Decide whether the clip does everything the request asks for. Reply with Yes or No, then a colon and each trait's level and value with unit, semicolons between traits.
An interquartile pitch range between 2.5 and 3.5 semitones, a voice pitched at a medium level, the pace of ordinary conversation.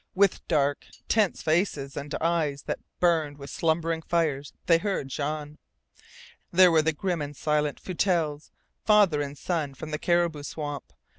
Yes: average, 2.8 semitones; medium, 155 Hz; average, 150 wpm